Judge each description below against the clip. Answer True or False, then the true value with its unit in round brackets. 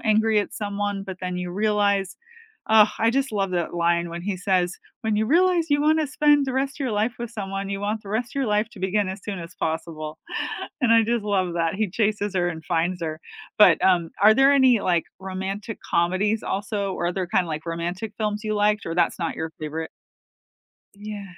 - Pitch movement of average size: True (3.6 semitones)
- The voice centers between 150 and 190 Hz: False (200 Hz)